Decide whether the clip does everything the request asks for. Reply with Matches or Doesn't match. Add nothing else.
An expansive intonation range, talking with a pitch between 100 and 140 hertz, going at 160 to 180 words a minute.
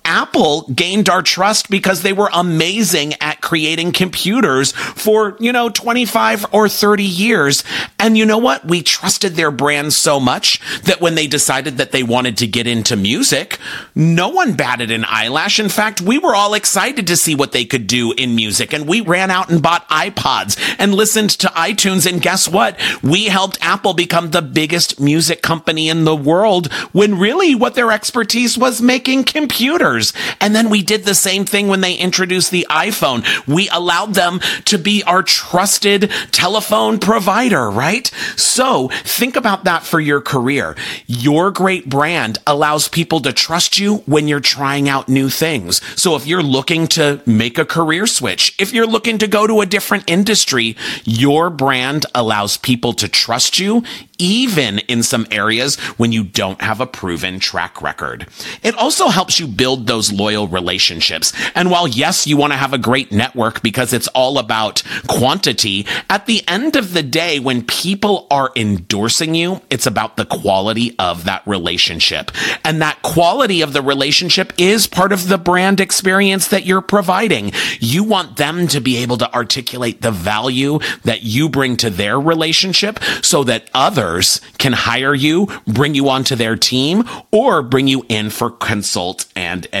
Doesn't match